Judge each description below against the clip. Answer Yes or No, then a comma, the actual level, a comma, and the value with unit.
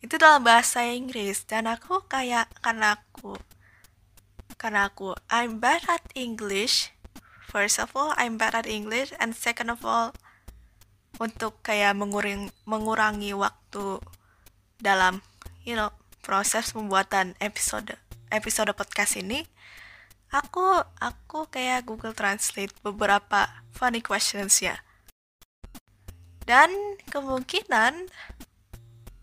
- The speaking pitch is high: Yes, high, 210 Hz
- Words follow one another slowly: No, average, 105 wpm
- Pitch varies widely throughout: No, average, 3.9 semitones